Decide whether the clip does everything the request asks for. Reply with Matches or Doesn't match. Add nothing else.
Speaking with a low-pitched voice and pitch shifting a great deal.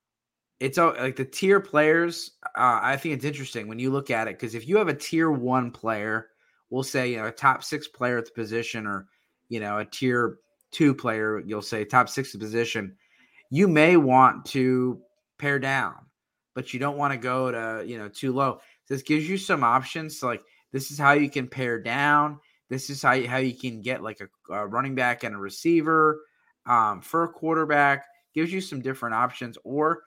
Doesn't match